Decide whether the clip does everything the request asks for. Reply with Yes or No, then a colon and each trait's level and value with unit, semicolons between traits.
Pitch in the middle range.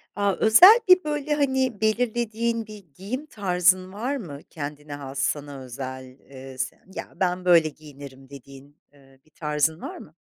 Yes: medium, 170 Hz